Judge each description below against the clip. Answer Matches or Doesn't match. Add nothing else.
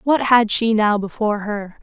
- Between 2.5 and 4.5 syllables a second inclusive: Doesn't match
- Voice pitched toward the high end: Matches